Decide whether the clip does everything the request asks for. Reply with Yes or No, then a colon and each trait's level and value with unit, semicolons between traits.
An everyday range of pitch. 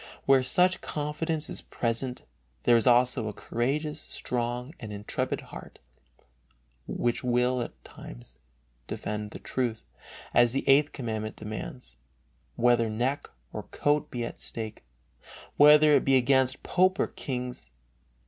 Yes: average, 3.4 semitones